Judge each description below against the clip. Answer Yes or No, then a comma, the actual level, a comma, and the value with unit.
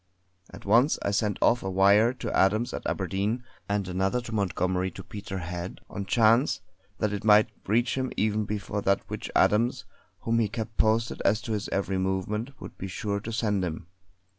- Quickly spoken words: No, average, 190 wpm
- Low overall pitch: Yes, low, 105 Hz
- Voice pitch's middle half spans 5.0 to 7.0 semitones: No, average, 2.8 semitones